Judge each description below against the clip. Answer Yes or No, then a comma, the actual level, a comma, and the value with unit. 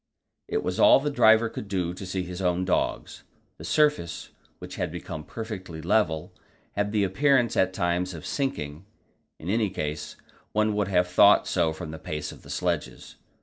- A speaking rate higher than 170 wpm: Yes, average, 180 wpm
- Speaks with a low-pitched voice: Yes, very low, 95 Hz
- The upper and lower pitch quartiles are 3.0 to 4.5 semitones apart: Yes, average, 4.0 semitones